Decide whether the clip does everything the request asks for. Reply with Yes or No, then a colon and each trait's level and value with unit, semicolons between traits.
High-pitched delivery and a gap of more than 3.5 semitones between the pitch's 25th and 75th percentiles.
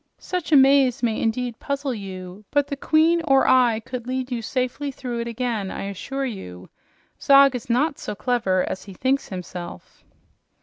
Yes: very high, 250 Hz; average, 4.4 semitones